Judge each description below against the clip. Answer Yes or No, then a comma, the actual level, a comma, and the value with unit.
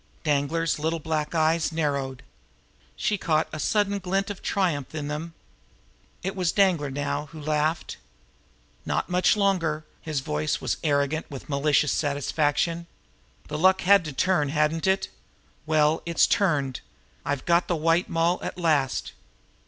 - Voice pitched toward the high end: No, medium, 155 Hz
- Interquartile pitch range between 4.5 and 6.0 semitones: No, average, 2.7 semitones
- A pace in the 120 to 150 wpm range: Yes, average, 145 wpm